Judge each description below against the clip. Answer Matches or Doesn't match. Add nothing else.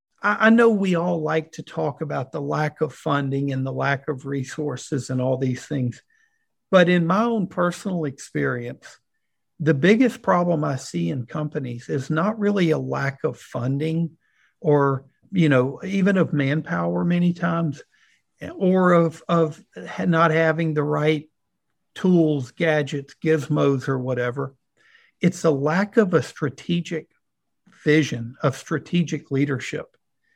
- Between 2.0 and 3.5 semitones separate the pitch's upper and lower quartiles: Doesn't match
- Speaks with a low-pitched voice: Doesn't match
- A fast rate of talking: Doesn't match